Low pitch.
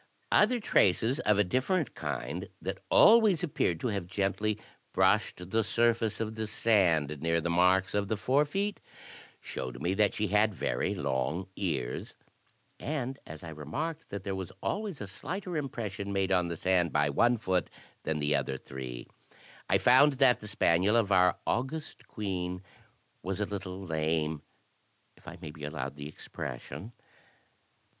Yes: low, 100 Hz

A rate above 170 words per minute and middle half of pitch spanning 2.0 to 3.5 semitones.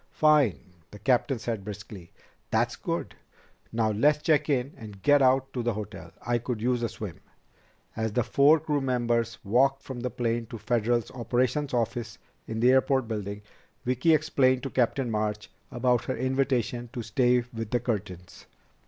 No: average, 165 wpm; average, 2.9 semitones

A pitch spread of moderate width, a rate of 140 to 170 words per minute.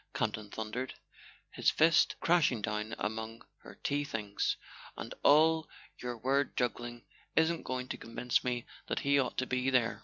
Yes: average, 3.9 semitones; average, 155 wpm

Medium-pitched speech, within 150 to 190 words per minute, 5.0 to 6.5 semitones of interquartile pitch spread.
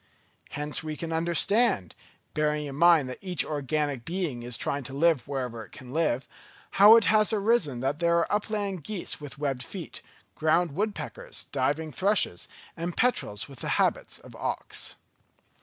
Yes: medium, 155 Hz; average, 160 wpm; wide, 5.4 semitones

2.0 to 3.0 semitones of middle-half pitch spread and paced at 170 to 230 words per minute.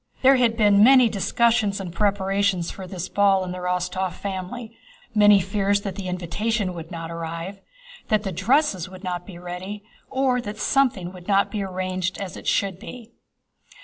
Yes: average, 2.7 semitones; average, 175 wpm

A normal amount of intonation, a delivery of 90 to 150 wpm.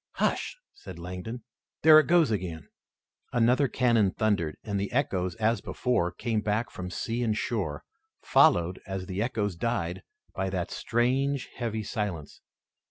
Yes: average, 4.7 semitones; average, 145 wpm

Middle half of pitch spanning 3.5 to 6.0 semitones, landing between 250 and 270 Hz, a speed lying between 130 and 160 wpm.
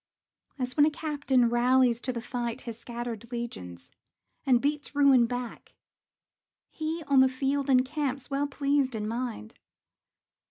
No: average, 2.8 semitones; very high, 255 Hz; slow, 135 wpm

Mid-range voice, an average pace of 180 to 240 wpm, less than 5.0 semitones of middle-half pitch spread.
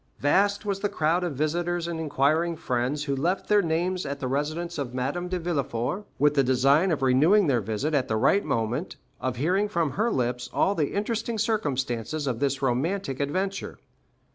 No: medium, 155 Hz; average, 190 wpm; wide, 5.4 semitones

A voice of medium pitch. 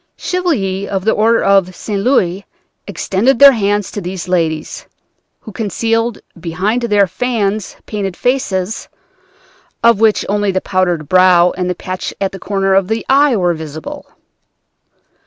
No: high, 195 Hz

